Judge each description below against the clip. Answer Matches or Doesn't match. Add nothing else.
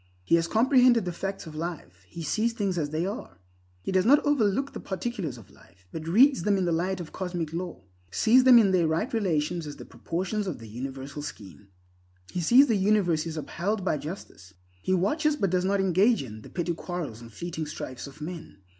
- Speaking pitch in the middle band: Matches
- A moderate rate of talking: Doesn't match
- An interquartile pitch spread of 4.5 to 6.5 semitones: Matches